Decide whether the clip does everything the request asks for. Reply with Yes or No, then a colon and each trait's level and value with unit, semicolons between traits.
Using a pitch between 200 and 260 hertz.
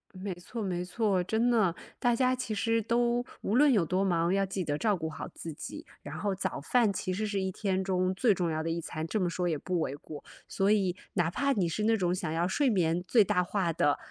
No: high, 190 Hz